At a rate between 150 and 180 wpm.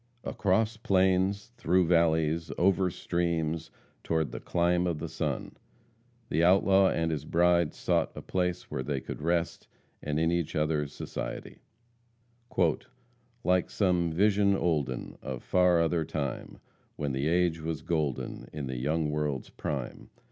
No: average, 140 wpm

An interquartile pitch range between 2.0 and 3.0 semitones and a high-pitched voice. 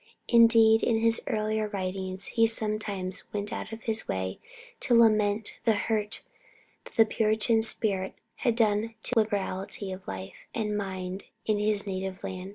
Yes: narrow, 2.6 semitones; high, 210 Hz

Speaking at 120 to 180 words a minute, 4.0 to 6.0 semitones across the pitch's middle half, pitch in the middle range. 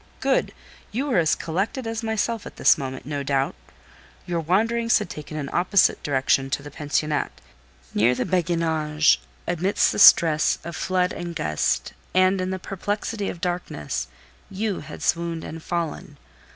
Yes: average, 155 wpm; average, 4.4 semitones; medium, 170 Hz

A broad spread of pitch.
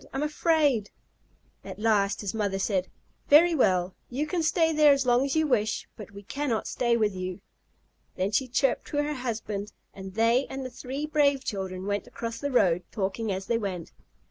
Yes: wide, 5.9 semitones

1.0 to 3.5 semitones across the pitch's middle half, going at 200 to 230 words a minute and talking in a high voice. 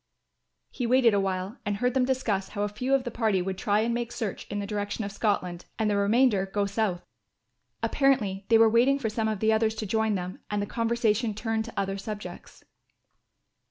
Yes: narrow, 2.6 semitones; fast, 205 wpm; high, 215 Hz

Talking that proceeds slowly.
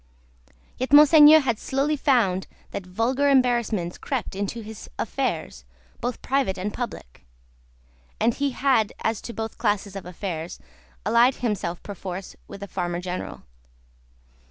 Yes: slow, 130 wpm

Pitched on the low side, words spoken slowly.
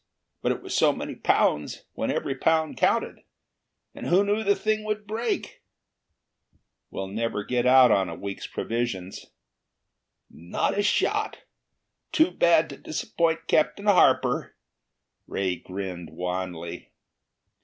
Yes: low, 130 Hz; slow, 125 wpm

